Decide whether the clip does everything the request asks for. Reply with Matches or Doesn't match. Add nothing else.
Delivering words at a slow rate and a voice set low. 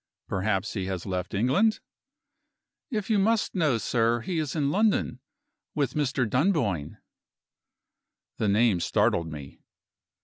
Matches